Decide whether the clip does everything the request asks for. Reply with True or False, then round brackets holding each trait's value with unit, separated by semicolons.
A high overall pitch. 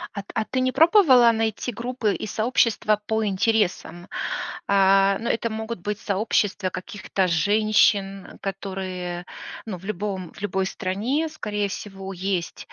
True (205 Hz)